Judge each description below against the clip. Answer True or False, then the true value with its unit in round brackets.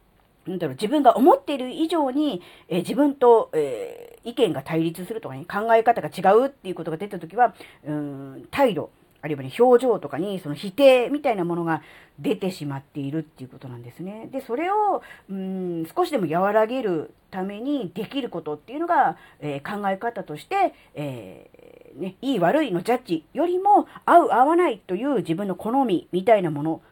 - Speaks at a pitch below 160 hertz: False (205 Hz)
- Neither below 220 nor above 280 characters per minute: False (355 characters per minute)